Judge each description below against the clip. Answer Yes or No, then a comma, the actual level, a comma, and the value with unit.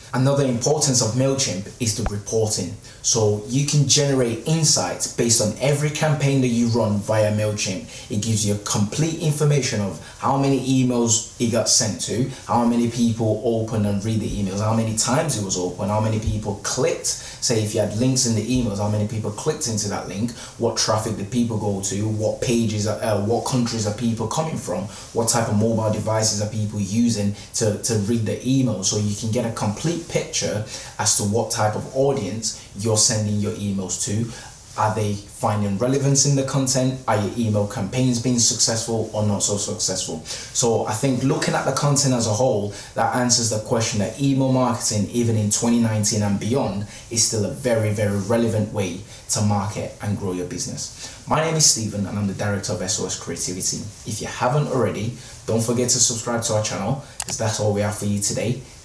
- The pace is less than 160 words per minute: No, average, 200 wpm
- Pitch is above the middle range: No, low, 115 Hz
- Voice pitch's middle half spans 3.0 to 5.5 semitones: Yes, average, 3.3 semitones